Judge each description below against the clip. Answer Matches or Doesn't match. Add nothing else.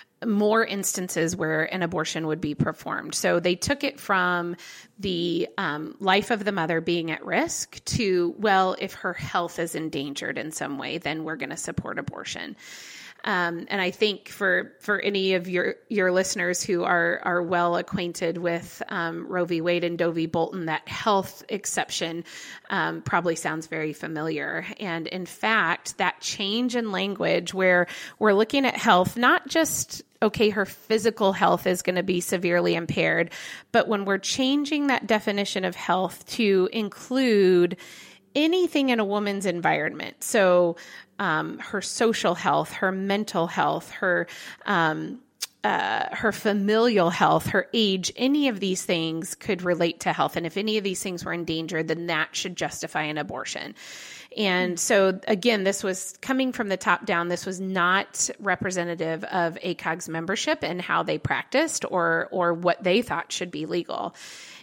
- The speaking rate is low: Doesn't match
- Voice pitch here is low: Doesn't match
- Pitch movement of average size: Matches